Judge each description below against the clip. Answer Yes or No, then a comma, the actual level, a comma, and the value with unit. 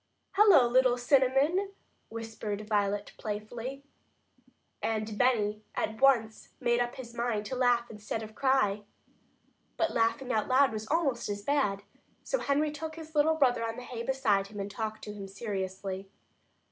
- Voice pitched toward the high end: Yes, high, 235 Hz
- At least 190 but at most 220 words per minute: No, average, 155 wpm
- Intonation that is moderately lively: Yes, average, 4.2 semitones